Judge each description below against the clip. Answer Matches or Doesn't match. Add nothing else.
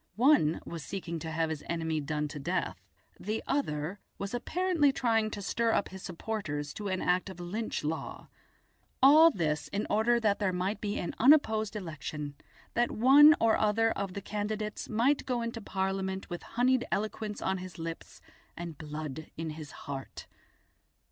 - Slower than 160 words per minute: Doesn't match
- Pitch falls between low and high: Doesn't match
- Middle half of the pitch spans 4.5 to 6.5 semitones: Matches